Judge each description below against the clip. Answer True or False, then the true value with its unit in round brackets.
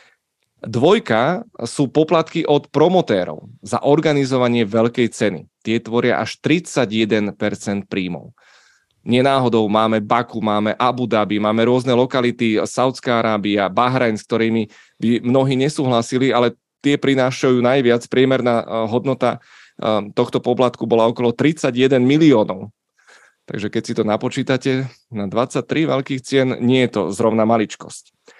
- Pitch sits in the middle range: False (120 Hz)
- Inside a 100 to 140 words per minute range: True (120 wpm)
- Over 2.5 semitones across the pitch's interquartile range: True (2.9 semitones)